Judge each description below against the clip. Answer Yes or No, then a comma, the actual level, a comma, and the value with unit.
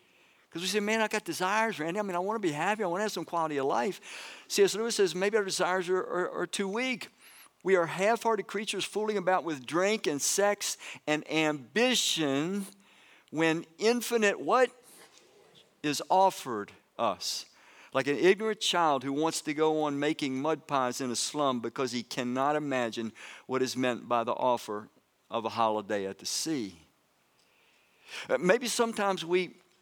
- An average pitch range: No, wide, 6.4 semitones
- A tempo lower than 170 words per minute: No, average, 175 wpm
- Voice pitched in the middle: Yes, medium, 175 Hz